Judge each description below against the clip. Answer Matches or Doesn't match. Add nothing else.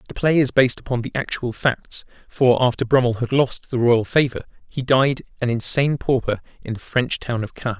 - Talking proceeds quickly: Matches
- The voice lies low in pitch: Matches